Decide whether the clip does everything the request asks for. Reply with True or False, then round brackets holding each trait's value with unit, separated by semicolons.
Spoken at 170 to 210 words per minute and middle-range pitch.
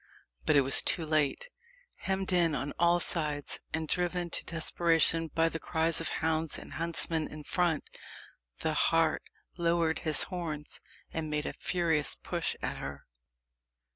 False (150 wpm; 165 Hz)